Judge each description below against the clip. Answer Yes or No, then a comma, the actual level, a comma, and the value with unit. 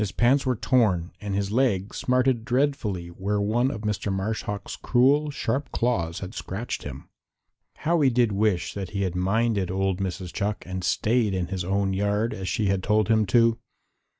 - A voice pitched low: Yes, low, 105 Hz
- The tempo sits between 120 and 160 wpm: No, average, 185 wpm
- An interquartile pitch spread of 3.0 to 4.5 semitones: Yes, average, 3.9 semitones